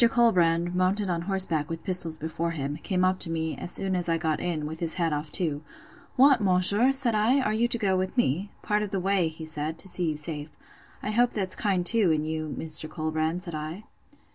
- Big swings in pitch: No, average, 4.0 semitones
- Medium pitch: Yes, medium, 175 Hz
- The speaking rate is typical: No, fast, 220 wpm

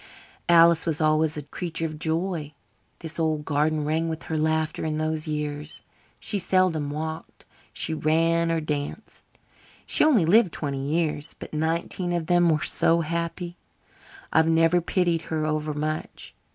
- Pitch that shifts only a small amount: Yes, narrow, 1.5 semitones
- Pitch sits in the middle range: Yes, medium, 160 Hz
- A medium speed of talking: Yes, average, 150 wpm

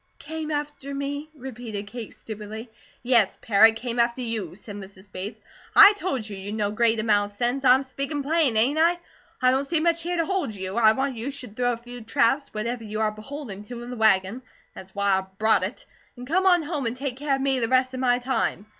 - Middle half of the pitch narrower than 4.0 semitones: No, average, 4.4 semitones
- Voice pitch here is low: No, high, 245 Hz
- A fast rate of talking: Yes, fast, 225 wpm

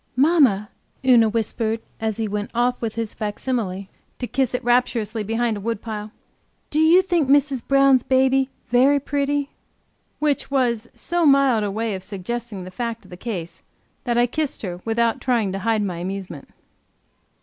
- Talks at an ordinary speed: Yes, average, 160 wpm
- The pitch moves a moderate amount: Yes, average, 4.1 semitones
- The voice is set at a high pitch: Yes, high, 235 Hz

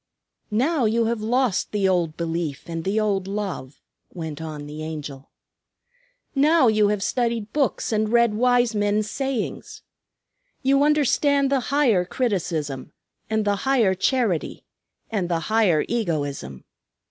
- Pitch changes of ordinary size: No, wide, 6.3 semitones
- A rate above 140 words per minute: No, slow, 135 wpm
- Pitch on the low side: No, high, 210 Hz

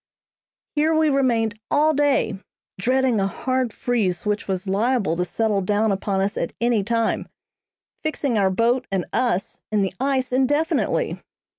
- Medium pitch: No, high, 230 Hz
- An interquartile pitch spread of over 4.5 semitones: Yes, average, 4.9 semitones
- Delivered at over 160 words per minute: No, average, 150 wpm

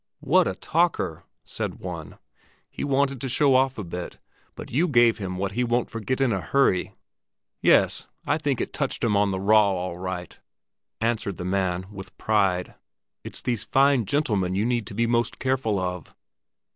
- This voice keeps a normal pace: Yes, average, 180 wpm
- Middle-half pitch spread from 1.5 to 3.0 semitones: No, wide, 5.6 semitones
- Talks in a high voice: No, low, 110 Hz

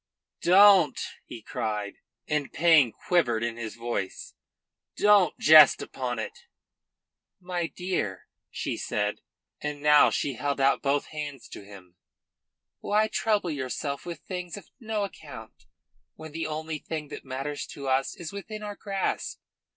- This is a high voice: No, medium, 150 Hz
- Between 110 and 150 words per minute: Yes, average, 140 wpm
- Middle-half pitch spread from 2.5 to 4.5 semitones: No, wide, 5.4 semitones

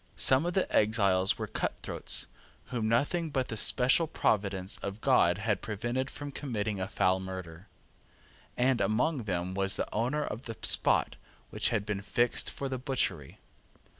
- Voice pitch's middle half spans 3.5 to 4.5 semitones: No, average, 5.1 semitones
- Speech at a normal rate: Yes, average, 160 wpm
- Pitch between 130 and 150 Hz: No, low, 110 Hz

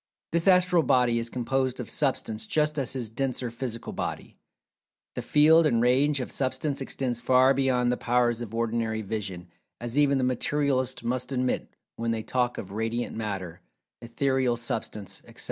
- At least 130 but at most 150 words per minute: No, average, 165 wpm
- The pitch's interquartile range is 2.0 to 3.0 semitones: Yes, average, 2.7 semitones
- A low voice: Yes, low, 125 Hz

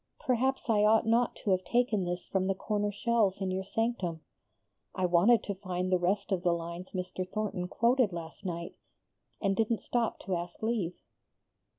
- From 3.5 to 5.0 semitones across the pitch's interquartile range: Yes, average, 3.8 semitones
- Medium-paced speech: Yes, average, 180 wpm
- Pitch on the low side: No, high, 195 Hz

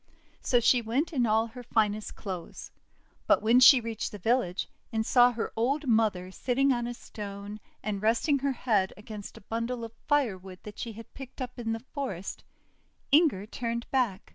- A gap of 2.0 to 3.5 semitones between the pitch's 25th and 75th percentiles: Yes, average, 3.0 semitones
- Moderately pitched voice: No, high, 230 Hz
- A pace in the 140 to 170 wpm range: No, average, 180 wpm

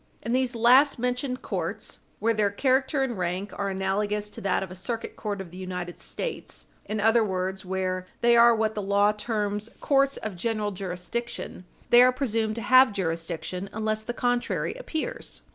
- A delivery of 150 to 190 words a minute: Yes, average, 180 wpm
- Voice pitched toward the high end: Yes, high, 215 Hz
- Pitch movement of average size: Yes, average, 3.9 semitones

